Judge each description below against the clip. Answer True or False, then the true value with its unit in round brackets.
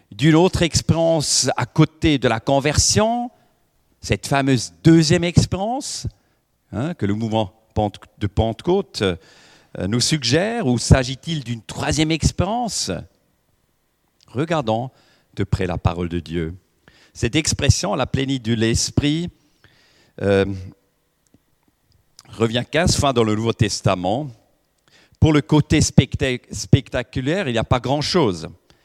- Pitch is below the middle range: True (125 Hz)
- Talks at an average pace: False (115 wpm)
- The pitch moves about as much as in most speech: False (6.0 semitones)